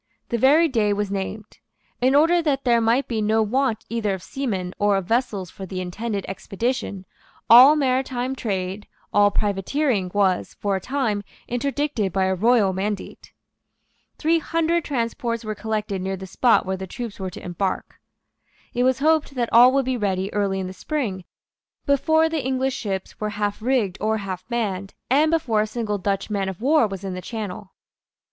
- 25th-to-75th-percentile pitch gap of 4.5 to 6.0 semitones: Yes, average, 5.1 semitones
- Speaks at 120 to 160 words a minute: No, average, 180 wpm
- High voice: Yes, high, 220 Hz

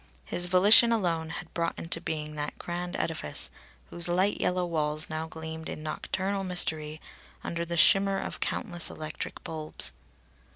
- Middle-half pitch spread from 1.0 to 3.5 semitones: Yes, narrow, 2.4 semitones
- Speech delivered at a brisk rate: No, average, 150 wpm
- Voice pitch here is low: No, medium, 170 Hz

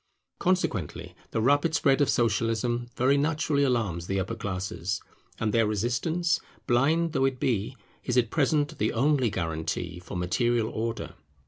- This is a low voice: Yes, low, 120 Hz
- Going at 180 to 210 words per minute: No, average, 150 wpm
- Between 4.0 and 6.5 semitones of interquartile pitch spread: Yes, average, 5.2 semitones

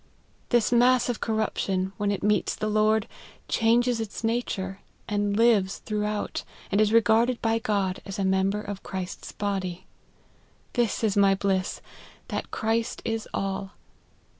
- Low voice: No, high, 210 Hz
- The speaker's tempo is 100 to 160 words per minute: Yes, average, 140 wpm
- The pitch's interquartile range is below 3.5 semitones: Yes, narrow, 2.5 semitones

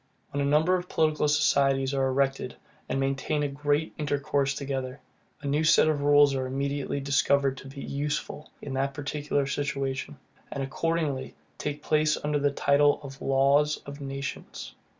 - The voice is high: No, medium, 140 Hz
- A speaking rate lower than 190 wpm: Yes, average, 160 wpm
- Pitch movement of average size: No, narrow, 1.3 semitones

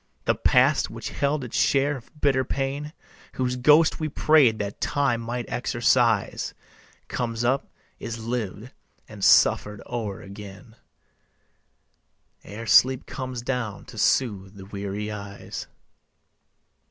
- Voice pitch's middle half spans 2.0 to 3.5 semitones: No, average, 4.0 semitones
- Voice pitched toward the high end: No, low, 120 Hz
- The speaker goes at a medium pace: No, slow, 120 wpm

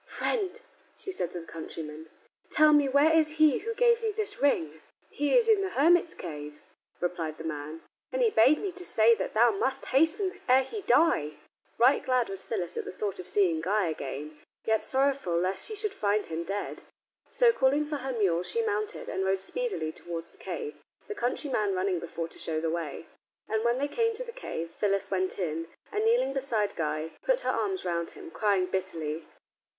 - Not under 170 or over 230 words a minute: Yes, average, 200 wpm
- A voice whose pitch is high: Yes, high, 220 Hz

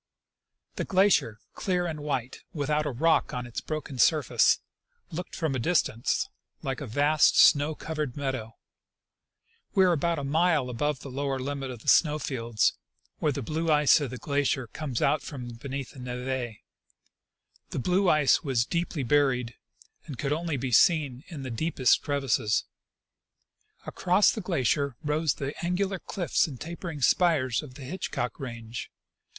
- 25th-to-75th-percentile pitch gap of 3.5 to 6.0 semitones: Yes, average, 3.9 semitones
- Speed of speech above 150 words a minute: Yes, average, 165 wpm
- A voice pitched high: No, medium, 145 Hz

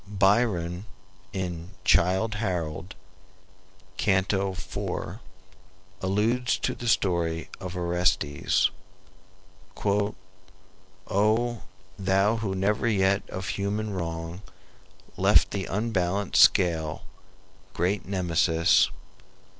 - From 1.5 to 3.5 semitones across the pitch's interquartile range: Yes, average, 2.7 semitones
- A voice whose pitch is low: Yes, very low, 95 Hz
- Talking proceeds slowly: Yes, slow, 80 wpm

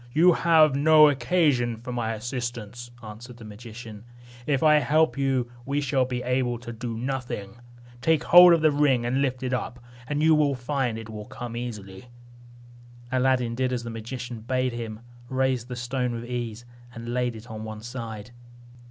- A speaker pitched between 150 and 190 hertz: No, low, 125 Hz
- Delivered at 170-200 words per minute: Yes, average, 175 wpm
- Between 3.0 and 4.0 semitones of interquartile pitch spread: No, narrow, 2.6 semitones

